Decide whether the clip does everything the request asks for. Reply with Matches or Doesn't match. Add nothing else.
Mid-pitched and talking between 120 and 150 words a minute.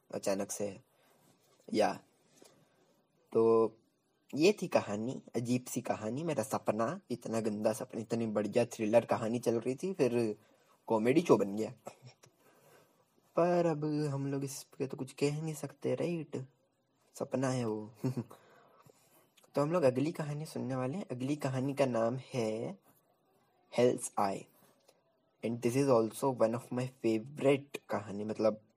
Doesn't match